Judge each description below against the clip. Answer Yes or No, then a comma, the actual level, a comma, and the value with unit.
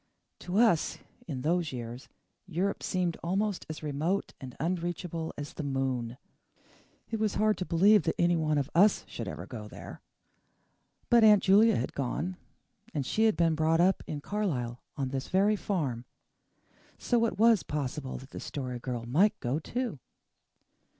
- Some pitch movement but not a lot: No, wide, 6.6 semitones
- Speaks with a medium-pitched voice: Yes, medium, 165 Hz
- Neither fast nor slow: Yes, average, 160 wpm